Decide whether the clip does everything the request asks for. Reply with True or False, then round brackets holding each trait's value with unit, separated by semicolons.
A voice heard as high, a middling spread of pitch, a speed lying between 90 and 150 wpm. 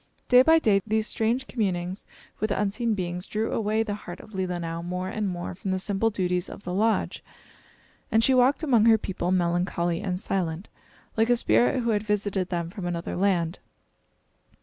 False (195 Hz; 3.8 semitones; 180 wpm)